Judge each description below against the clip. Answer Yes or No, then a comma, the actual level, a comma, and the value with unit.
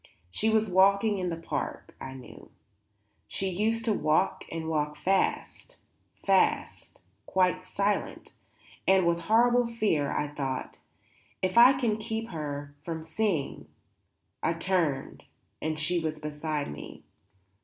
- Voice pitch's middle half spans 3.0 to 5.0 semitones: No, wide, 5.6 semitones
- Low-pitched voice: No, medium, 180 Hz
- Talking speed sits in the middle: No, slow, 130 wpm